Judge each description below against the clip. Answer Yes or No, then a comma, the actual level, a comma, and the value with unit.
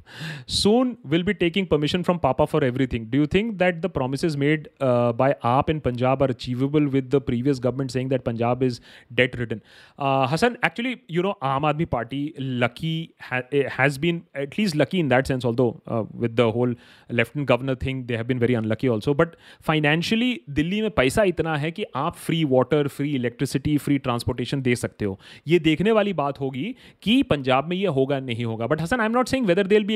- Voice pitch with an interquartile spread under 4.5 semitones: No, average, 4.8 semitones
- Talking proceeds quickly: Yes, fast, 205 wpm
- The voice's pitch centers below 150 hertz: Yes, medium, 140 Hz